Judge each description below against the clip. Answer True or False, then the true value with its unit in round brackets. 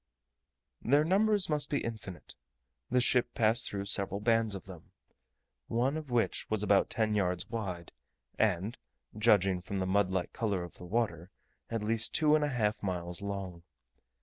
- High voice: False (105 Hz)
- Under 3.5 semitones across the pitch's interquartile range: False (3.9 semitones)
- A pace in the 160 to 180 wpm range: True (165 wpm)